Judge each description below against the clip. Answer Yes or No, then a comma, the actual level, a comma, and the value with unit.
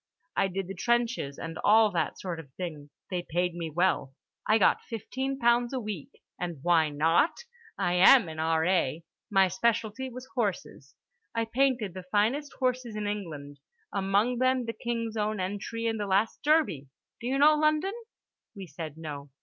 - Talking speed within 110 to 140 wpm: No, average, 170 wpm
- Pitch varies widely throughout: Yes, wide, 5.9 semitones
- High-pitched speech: Yes, high, 205 Hz